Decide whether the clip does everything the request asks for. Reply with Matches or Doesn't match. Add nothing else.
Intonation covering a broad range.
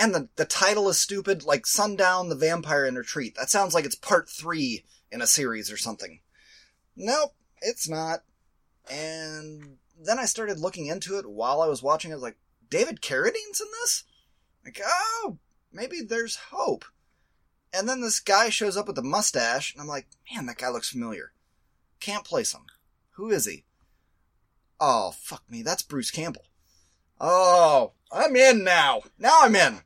Matches